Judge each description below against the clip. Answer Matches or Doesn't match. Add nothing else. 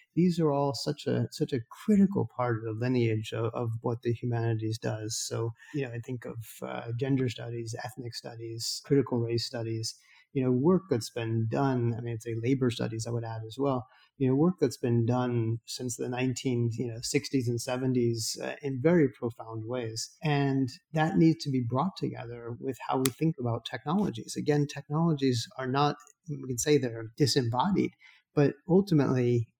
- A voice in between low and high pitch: Doesn't match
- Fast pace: Doesn't match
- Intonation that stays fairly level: Doesn't match